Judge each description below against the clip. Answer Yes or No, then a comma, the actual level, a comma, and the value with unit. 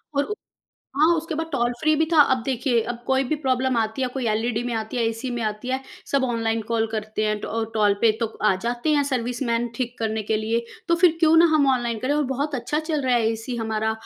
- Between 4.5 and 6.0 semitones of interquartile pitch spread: No, average, 3.6 semitones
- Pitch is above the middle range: Yes, high, 240 Hz